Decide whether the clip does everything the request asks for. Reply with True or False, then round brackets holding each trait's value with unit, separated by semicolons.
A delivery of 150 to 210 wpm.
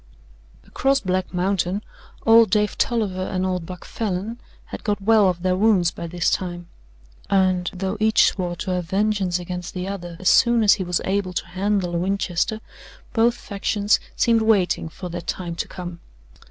True (175 wpm)